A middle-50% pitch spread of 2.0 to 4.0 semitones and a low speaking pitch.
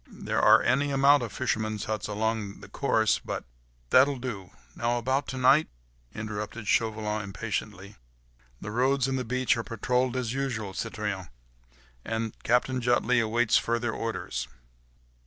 Yes: average, 3.1 semitones; low, 115 Hz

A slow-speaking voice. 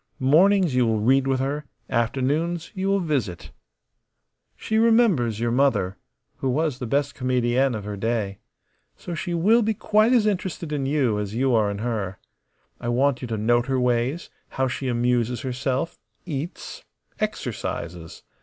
No: average, 160 wpm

